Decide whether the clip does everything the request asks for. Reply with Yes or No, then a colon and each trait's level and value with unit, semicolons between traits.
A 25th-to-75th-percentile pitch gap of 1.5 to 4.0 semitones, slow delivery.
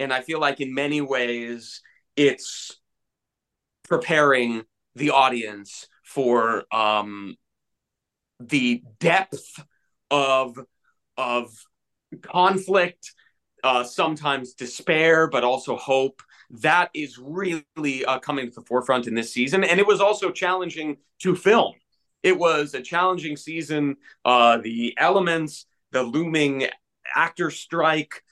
No: average, 4.7 semitones; slow, 115 wpm